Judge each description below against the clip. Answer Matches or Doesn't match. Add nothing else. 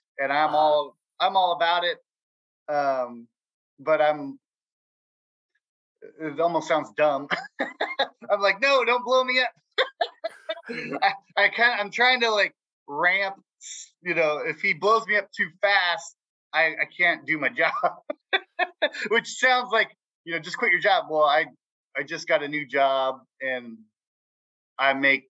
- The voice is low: Doesn't match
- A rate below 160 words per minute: Matches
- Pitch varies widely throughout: Matches